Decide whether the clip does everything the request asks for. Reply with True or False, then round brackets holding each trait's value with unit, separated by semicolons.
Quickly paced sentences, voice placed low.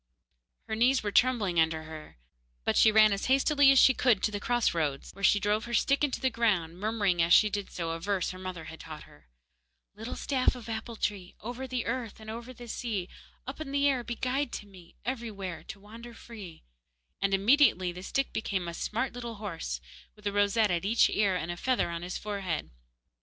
False (215 wpm; 210 Hz)